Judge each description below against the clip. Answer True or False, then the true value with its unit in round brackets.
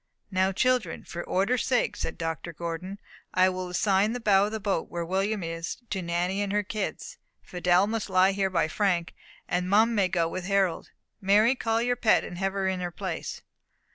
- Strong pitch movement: False (2.8 semitones)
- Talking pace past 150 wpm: True (200 wpm)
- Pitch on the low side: False (190 Hz)